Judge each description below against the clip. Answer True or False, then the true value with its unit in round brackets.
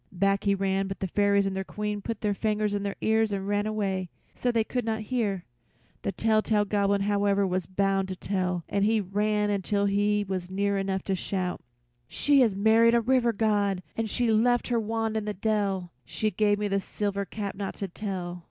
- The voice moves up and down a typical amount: False (1.8 semitones)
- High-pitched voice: True (205 Hz)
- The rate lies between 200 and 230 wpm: True (205 wpm)